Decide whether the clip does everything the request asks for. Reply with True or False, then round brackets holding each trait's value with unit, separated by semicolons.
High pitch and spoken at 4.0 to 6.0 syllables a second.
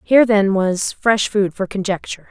True (200 Hz; 5.0 syllables/s)